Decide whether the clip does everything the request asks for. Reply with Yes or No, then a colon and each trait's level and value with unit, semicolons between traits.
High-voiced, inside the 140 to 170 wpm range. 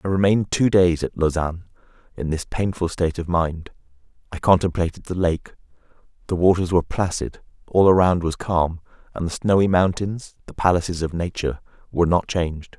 No: very low, 90 Hz; average, 165 wpm